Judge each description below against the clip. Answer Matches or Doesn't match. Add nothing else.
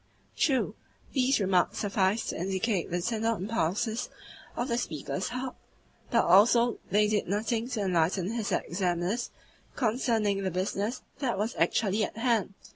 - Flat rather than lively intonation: Doesn't match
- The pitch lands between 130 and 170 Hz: Doesn't match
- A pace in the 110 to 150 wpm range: Matches